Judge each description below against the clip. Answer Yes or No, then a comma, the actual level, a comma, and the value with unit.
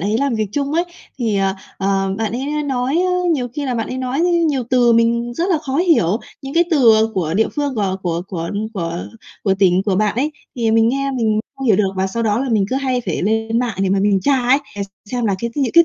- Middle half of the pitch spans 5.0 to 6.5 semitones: Yes, average, 5.3 semitones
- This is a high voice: Yes, high, 230 Hz